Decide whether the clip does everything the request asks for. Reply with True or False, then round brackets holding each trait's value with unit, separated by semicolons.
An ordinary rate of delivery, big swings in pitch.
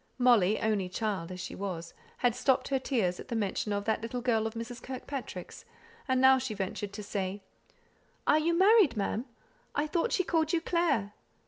False (190 wpm; 4.9 semitones)